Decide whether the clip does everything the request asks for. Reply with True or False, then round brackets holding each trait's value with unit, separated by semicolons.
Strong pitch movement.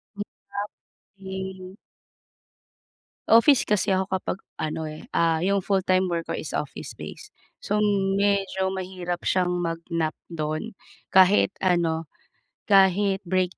False (2.5 semitones)